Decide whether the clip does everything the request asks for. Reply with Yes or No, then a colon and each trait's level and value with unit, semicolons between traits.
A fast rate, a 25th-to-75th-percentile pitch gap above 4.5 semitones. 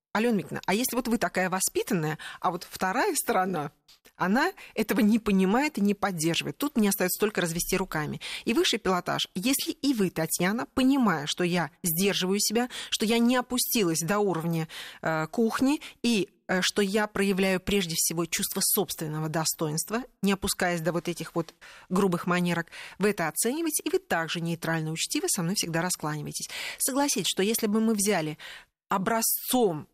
Yes: fast, 165 wpm; average, 5.0 semitones